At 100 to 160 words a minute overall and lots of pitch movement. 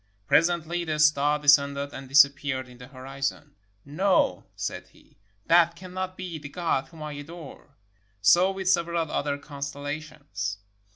No: average, 150 wpm; average, 3.4 semitones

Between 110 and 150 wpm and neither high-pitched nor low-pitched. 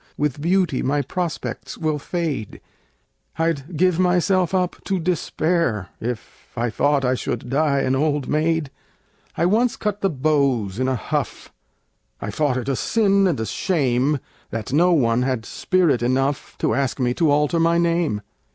No: average, 160 wpm; medium, 150 Hz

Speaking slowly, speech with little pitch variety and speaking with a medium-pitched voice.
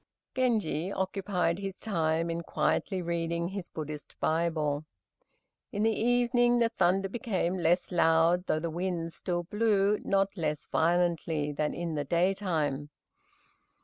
No: slow, 130 wpm; average, 3.2 semitones; medium, 175 Hz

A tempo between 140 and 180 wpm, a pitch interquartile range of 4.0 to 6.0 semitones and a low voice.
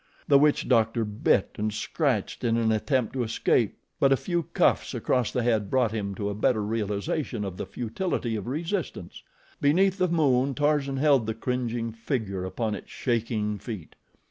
Yes: average, 170 wpm; average, 4.4 semitones; low, 115 Hz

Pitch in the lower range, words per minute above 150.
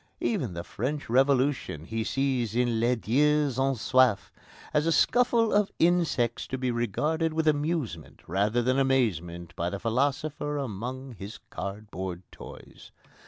No: low, 130 Hz; average, 140 wpm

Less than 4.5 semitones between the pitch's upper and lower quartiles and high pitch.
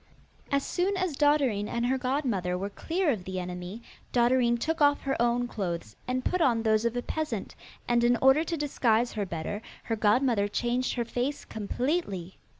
No: average, 5.0 semitones; high, 240 Hz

